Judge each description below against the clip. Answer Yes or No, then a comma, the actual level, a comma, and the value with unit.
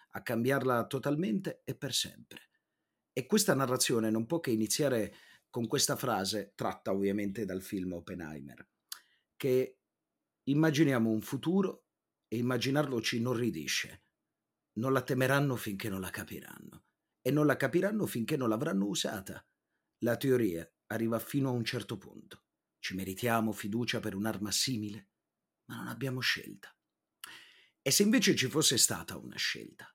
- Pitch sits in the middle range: No, low, 120 Hz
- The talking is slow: No, average, 140 wpm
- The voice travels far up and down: No, average, 4.6 semitones